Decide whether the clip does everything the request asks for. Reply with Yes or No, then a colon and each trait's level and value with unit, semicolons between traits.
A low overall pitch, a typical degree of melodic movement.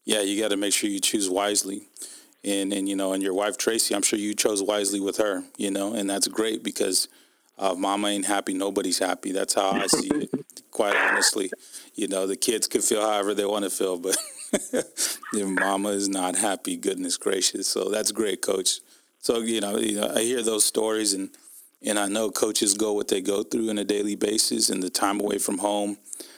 No: low, 105 Hz; narrow, 1.9 semitones